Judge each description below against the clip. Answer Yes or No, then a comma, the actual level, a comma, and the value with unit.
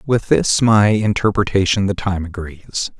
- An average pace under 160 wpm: Yes, average, 140 wpm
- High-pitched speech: No, low, 100 Hz